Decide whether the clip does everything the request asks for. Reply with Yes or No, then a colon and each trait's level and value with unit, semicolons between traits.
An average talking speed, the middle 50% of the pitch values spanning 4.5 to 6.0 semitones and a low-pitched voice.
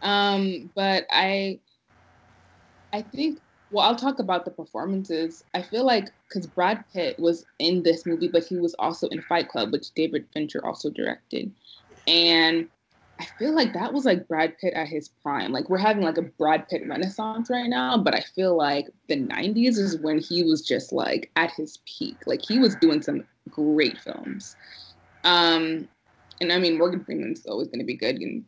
No: average, 190 wpm; average, 4.9 semitones; medium, 175 Hz